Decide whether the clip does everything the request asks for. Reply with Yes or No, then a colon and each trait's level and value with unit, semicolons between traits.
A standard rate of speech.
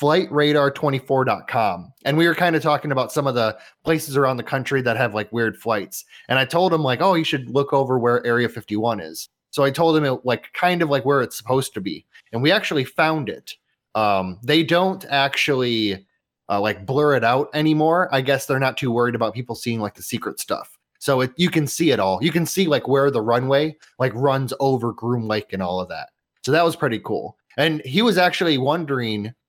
No: fast, 220 wpm